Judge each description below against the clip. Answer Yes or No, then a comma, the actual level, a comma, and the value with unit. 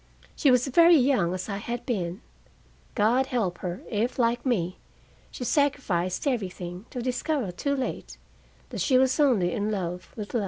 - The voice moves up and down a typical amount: No, wide, 6.0 semitones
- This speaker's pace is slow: No, average, 165 wpm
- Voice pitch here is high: Yes, high, 235 Hz